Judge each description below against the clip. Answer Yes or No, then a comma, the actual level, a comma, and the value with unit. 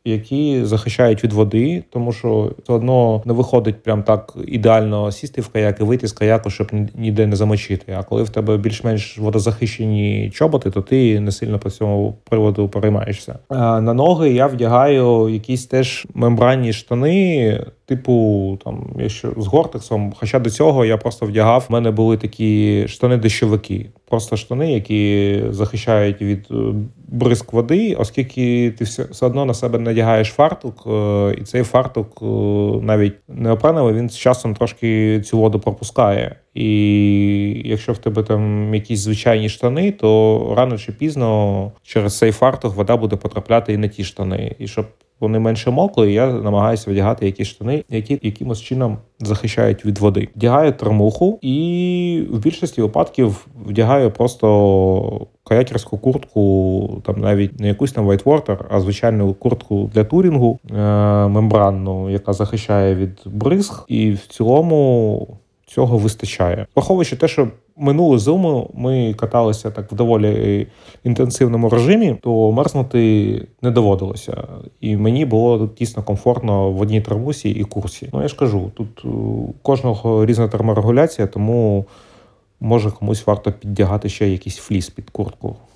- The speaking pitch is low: Yes, low, 110 Hz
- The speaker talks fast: No, average, 145 wpm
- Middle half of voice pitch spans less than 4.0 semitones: Yes, average, 2.9 semitones